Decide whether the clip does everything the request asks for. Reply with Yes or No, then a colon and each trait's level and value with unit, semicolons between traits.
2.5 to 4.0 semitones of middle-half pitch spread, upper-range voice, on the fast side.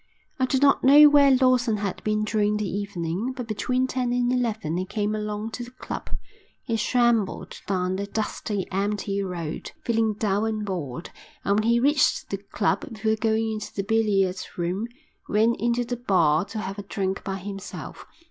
No: average, 3.4 semitones; high, 215 Hz; average, 180 wpm